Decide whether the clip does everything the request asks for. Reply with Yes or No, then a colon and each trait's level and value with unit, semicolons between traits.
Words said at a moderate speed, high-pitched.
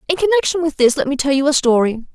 No: fast, 280 wpm; very high, 290 Hz